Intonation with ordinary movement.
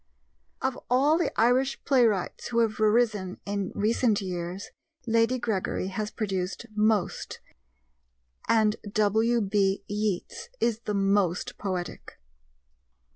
Yes: average, 3.0 semitones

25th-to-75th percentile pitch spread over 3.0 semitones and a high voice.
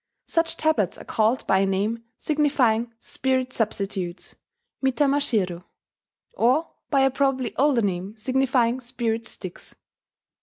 Yes: average, 4.1 semitones; high, 240 Hz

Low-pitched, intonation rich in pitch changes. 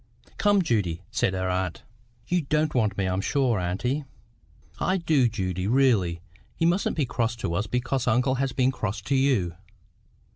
Yes: low, 120 Hz; wide, 6.4 semitones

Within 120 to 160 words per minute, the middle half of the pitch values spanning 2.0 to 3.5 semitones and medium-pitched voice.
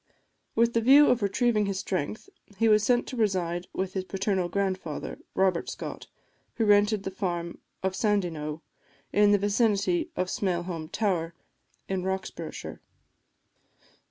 No: slow, 135 wpm; average, 2.9 semitones; high, 195 Hz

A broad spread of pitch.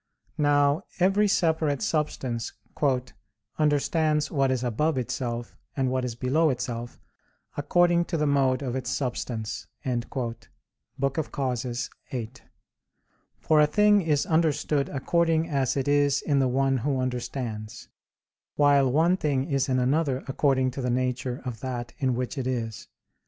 No: average, 3.2 semitones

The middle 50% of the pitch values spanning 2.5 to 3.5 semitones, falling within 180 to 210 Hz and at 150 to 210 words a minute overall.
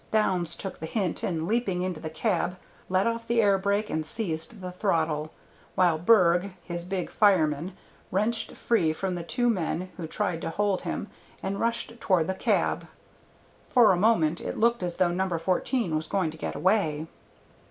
No: average, 4.0 semitones; medium, 185 Hz; average, 180 wpm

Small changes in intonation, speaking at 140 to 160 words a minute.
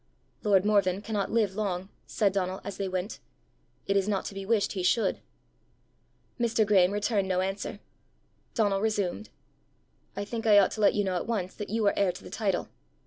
No: narrow, 1.9 semitones; average, 195 wpm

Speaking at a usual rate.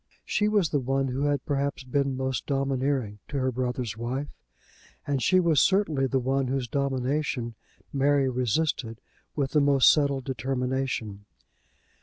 Yes: average, 145 wpm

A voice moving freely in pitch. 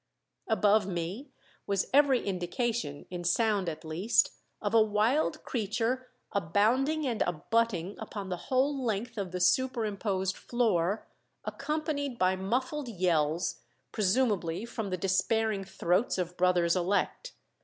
No: average, 4.8 semitones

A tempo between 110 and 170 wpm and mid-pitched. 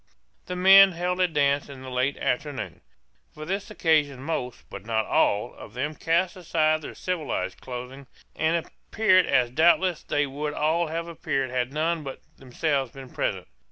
Yes: average, 165 wpm; medium, 150 Hz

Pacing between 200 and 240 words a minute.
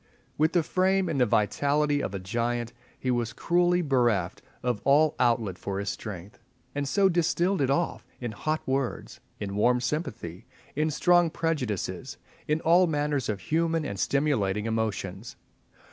No: average, 155 wpm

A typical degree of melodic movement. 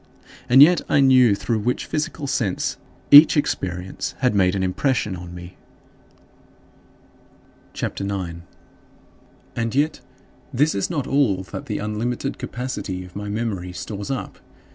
No: wide, 6.2 semitones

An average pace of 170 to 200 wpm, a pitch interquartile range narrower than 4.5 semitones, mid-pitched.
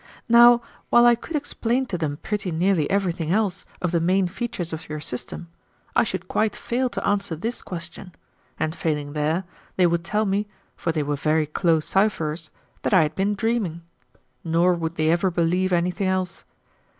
Yes: average, 180 wpm; average, 4.0 semitones; medium, 180 Hz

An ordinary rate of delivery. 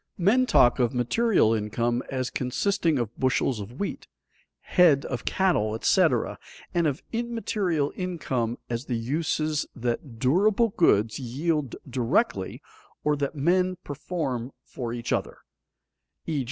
No: slow, 125 wpm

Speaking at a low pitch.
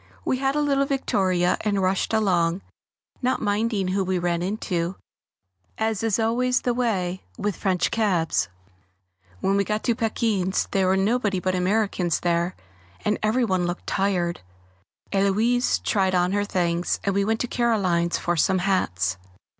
No: high, 195 Hz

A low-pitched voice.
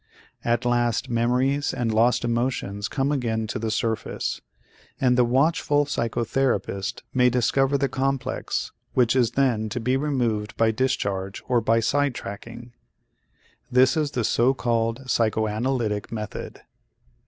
Yes: low, 120 Hz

